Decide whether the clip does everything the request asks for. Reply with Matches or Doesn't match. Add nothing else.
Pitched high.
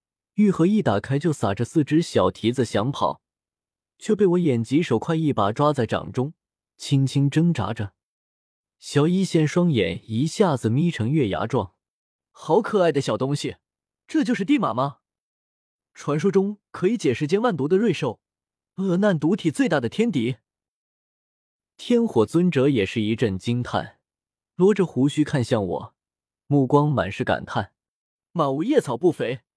Doesn't match